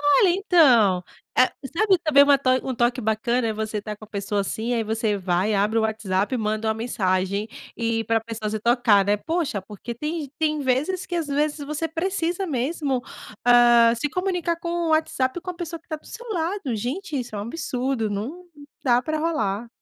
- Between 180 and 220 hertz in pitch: No, high, 245 Hz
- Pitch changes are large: Yes, wide, 6.4 semitones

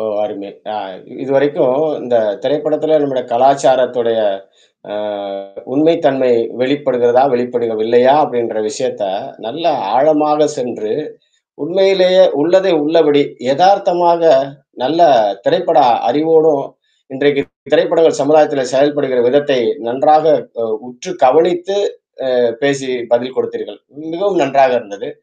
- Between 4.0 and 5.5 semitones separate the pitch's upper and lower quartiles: Yes, average, 4.3 semitones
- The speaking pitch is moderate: Yes, medium, 145 Hz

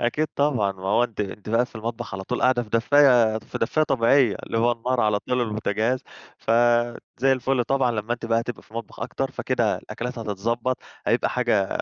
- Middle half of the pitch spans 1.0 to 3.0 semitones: Yes, narrow, 2.5 semitones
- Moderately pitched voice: No, low, 115 Hz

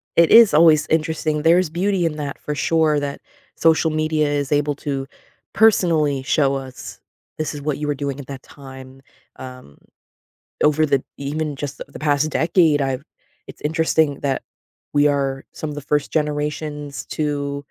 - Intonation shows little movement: Yes, narrow, 1.9 semitones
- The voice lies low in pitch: No, medium, 150 Hz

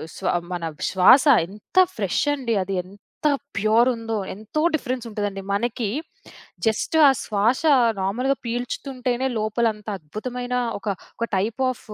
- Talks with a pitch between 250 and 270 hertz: No, high, 225 Hz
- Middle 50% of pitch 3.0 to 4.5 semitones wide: Yes, average, 3.4 semitones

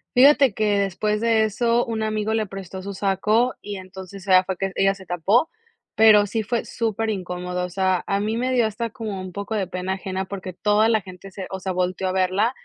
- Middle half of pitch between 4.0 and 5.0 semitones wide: No, average, 2.8 semitones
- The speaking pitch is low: No, high, 200 Hz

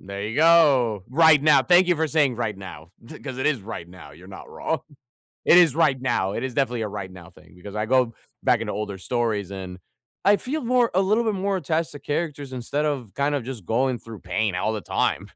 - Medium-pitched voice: No, low, 130 Hz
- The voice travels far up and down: Yes, wide, 7.2 semitones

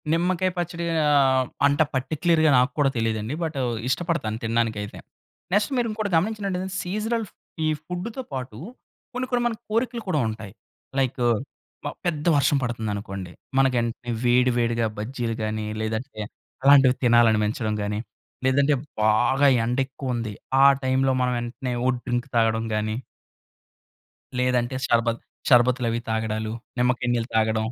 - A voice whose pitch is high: No, low, 125 Hz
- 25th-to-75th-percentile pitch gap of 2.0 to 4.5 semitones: No, average, 5.0 semitones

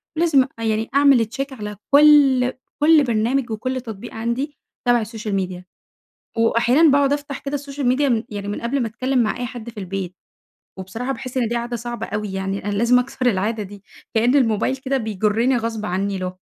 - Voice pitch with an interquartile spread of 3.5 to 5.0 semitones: Yes, average, 3.9 semitones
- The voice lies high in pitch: Yes, high, 235 Hz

